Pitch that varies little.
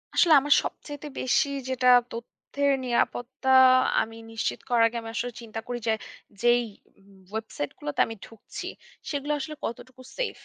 No: average, 3.7 semitones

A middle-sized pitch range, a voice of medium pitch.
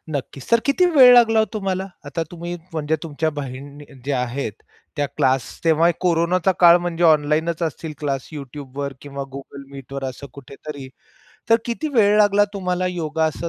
Yes: average, 4.4 semitones; medium, 160 Hz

